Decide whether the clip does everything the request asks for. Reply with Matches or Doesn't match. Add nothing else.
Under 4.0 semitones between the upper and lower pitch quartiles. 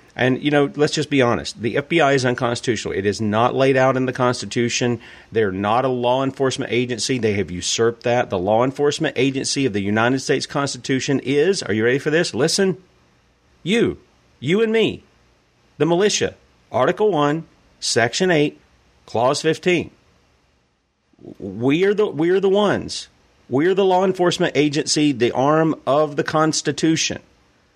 Doesn't match